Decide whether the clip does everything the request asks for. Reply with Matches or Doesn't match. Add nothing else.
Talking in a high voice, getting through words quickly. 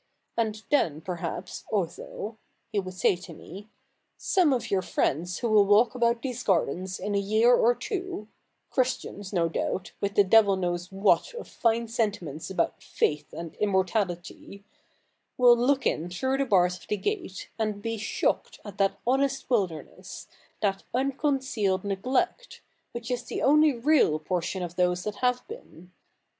Doesn't match